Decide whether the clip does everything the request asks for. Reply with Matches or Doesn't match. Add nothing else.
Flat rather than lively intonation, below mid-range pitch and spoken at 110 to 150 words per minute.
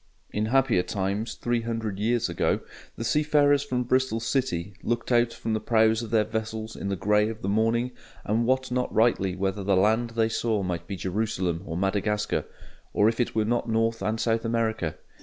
Doesn't match